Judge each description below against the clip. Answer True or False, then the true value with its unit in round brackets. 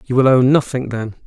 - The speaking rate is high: True (235 wpm)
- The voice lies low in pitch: True (125 Hz)